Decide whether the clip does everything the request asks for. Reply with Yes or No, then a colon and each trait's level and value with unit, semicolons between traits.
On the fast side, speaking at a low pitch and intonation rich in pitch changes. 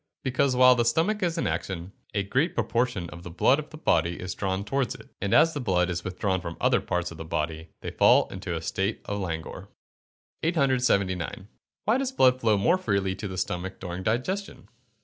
Yes: fast, 210 wpm; low, 100 Hz; wide, 6.8 semitones